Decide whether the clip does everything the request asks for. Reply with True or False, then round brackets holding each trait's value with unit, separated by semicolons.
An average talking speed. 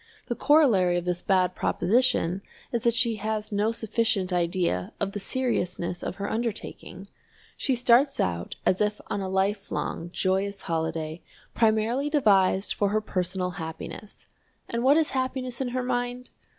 True (150 wpm)